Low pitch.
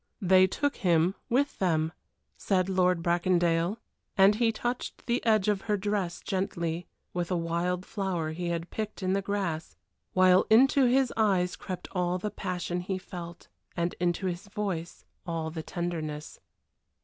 No: medium, 185 Hz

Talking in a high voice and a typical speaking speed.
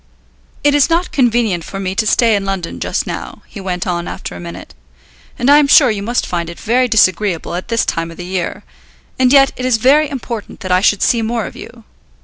No: high, 215 Hz; fast, 230 wpm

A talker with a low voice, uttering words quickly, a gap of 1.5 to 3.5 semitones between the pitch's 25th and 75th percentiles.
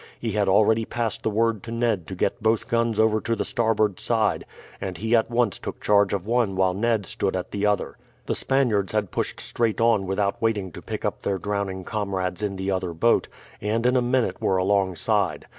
Yes: low, 105 Hz; fast, 210 wpm; average, 3.0 semitones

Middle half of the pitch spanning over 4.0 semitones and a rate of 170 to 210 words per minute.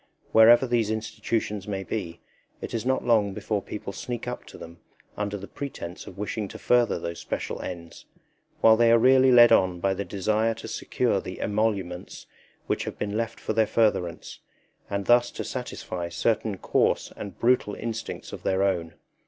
No: average, 3.2 semitones; average, 175 wpm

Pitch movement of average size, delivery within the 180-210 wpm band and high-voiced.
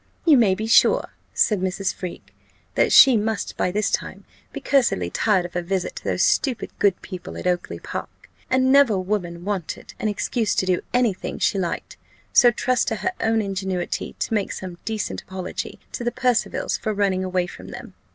Yes: average, 3.6 semitones; average, 190 wpm; high, 200 Hz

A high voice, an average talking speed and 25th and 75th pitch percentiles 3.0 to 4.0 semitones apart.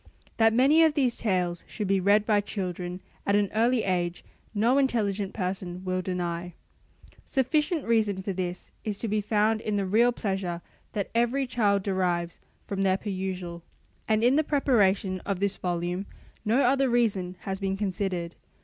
Yes: high, 200 Hz; average, 165 wpm; average, 3.7 semitones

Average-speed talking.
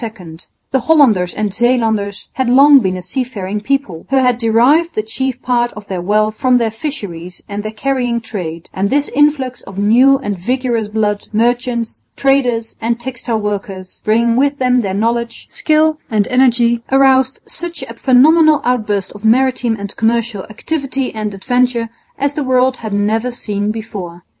Yes: average, 160 wpm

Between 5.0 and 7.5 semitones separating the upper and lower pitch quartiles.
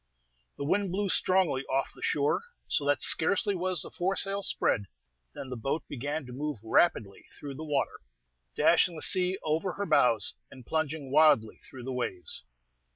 Yes: wide, 5.4 semitones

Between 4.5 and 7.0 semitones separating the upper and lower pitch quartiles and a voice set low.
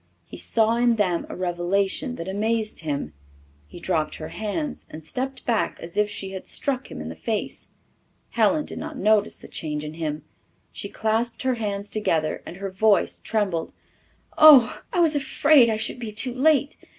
No: wide, 5.5 semitones; high, 215 Hz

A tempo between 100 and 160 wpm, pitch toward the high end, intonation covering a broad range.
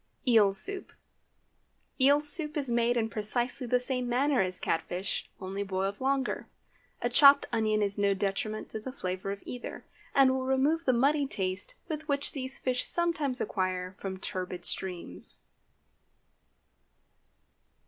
Yes: average, 140 wpm; high, 240 Hz; wide, 5.7 semitones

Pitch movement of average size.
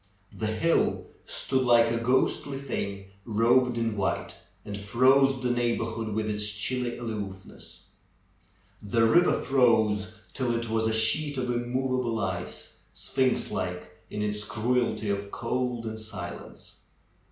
Yes: average, 3.1 semitones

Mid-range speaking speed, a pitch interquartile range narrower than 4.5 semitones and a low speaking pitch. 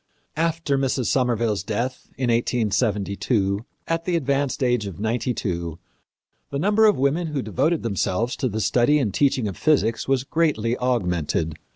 No: average, 155 wpm; average, 4.9 semitones; low, 125 Hz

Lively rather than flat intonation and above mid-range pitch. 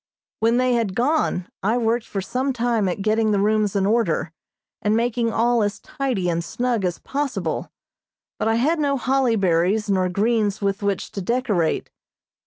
No: average, 3.6 semitones; high, 220 Hz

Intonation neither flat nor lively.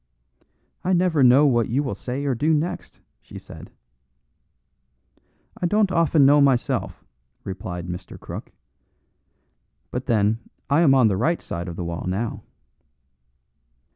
No: wide, 6.6 semitones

